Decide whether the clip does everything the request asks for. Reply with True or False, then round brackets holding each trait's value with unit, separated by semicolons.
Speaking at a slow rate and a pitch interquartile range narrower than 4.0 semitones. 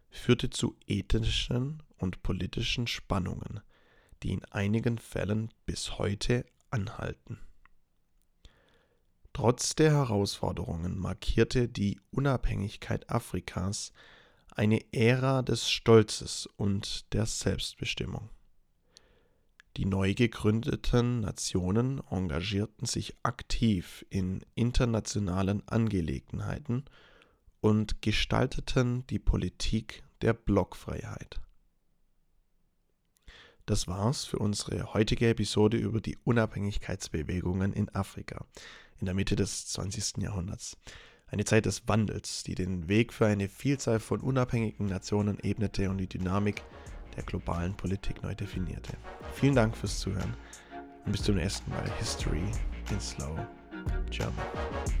True (105 wpm; 3.6 semitones)